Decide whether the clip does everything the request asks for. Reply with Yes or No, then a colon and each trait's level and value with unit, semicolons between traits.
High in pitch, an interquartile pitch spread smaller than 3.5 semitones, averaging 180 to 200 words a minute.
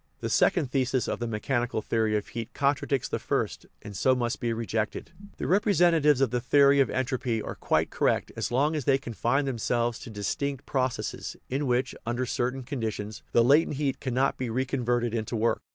No: low, 125 Hz; average, 2.9 semitones; average, 195 wpm